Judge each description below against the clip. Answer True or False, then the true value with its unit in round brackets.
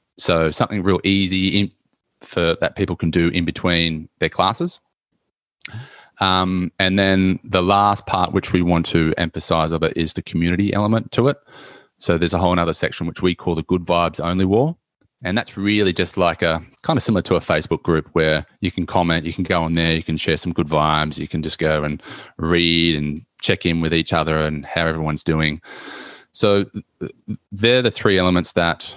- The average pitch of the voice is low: True (85 Hz)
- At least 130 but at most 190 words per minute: False (200 wpm)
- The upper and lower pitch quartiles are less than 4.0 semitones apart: True (2.9 semitones)